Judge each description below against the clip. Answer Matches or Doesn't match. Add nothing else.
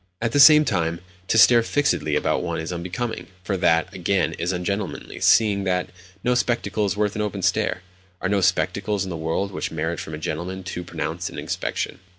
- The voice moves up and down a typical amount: Matches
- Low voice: Matches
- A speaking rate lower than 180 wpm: Doesn't match